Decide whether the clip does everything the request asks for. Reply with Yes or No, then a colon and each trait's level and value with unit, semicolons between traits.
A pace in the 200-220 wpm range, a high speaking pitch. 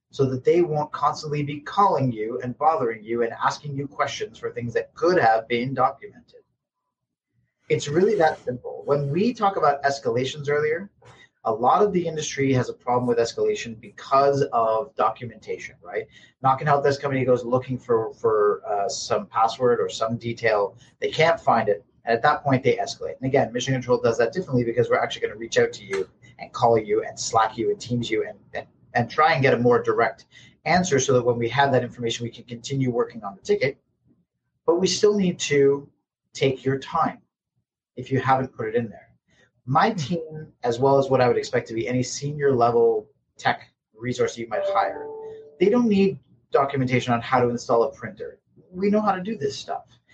No: fast, 205 wpm; medium, 140 Hz